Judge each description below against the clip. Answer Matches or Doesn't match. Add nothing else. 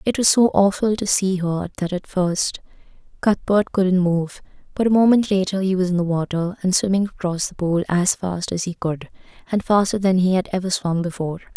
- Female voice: Matches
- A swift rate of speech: Matches